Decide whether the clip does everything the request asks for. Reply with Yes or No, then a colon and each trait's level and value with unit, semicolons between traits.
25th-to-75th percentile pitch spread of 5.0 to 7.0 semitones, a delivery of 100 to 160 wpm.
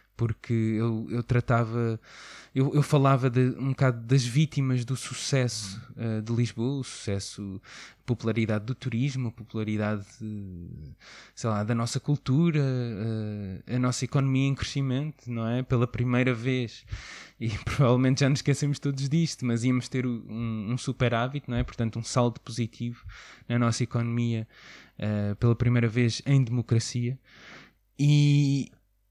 No: average, 2.7 semitones; average, 145 wpm